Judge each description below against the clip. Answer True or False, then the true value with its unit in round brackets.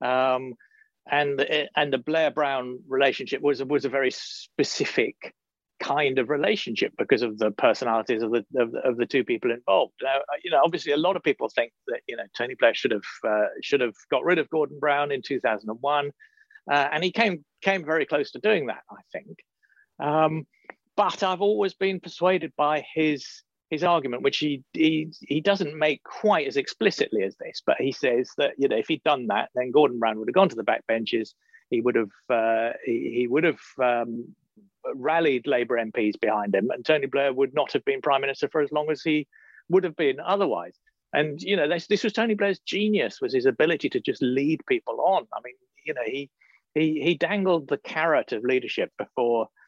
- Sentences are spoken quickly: True (210 wpm)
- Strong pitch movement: True (7.5 semitones)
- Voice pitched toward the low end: False (155 Hz)